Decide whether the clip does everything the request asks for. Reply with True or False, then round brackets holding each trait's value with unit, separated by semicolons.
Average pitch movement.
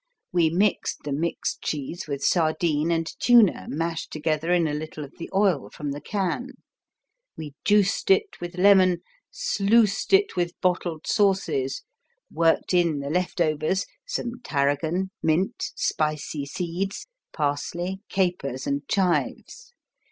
True (4.0 semitones)